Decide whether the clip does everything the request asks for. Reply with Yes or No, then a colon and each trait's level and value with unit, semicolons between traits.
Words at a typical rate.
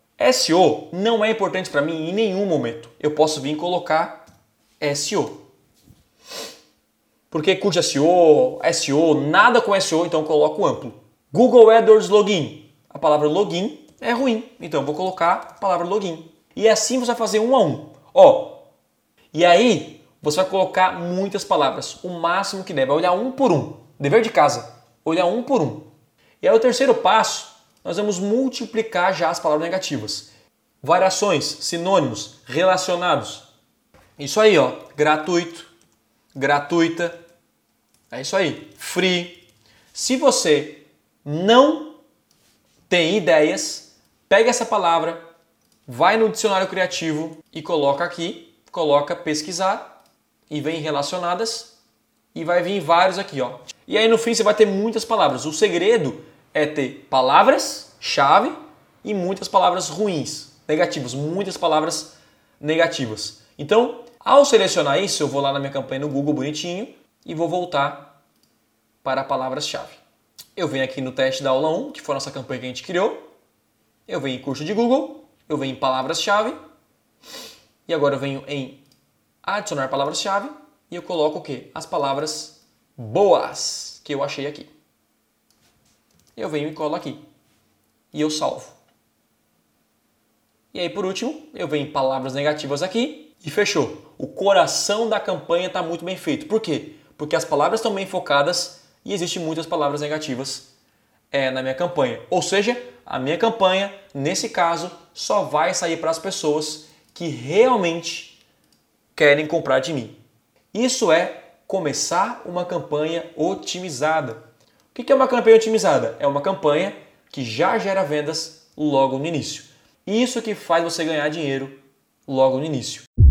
Yes: average, 150 wpm